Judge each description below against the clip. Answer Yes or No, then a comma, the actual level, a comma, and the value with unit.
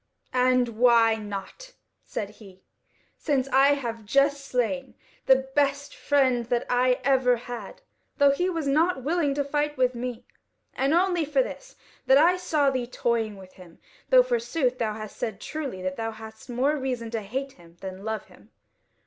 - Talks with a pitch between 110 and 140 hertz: No, very high, 255 Hz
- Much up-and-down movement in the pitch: No, average, 4.1 semitones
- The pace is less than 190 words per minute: Yes, average, 170 wpm